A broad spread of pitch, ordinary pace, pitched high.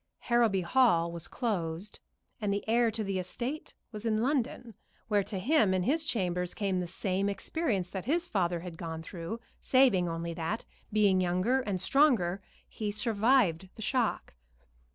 No: average, 4.8 semitones; average, 160 wpm; high, 200 Hz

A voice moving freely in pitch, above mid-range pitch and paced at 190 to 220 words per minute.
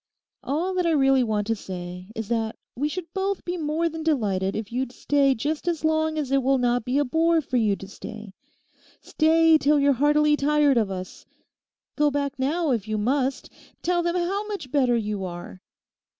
Yes: wide, 6.0 semitones; very high, 275 Hz; average, 195 wpm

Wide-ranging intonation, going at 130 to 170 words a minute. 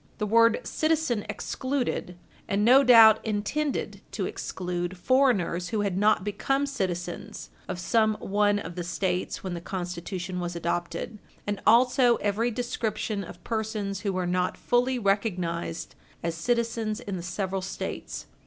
No: average, 4.4 semitones; average, 145 wpm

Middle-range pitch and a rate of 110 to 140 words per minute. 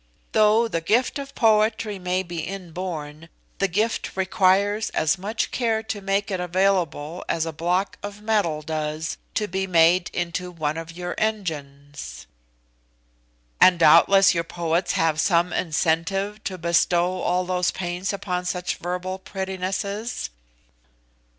Yes: medium, 180 Hz; slow, 135 wpm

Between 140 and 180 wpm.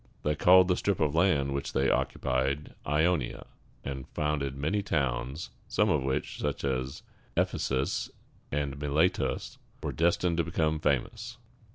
Yes: average, 150 wpm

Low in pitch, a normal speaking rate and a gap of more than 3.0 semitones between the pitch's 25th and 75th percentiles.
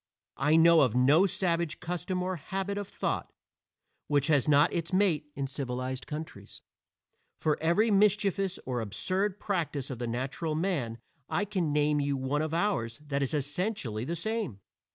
No: medium, 155 Hz; average, 160 wpm; average, 5.3 semitones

